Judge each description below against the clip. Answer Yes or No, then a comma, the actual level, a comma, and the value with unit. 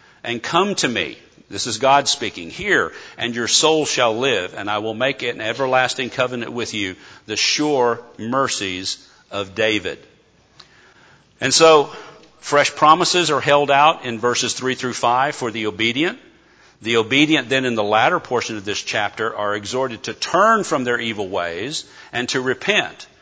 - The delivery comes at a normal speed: Yes, average, 170 wpm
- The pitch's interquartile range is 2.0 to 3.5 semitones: No, average, 4.2 semitones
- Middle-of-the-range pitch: No, low, 120 Hz